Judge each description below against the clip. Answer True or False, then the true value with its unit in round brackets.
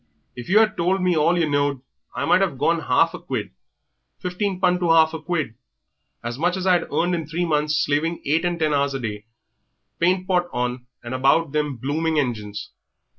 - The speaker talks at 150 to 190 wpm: False (200 wpm)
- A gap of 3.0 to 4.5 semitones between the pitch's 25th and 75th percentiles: True (4.2 semitones)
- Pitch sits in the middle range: True (160 Hz)